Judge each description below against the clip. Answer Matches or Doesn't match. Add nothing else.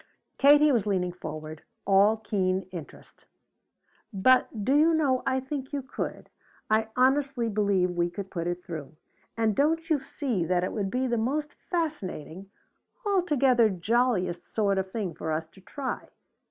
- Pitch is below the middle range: Doesn't match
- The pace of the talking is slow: Doesn't match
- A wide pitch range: Matches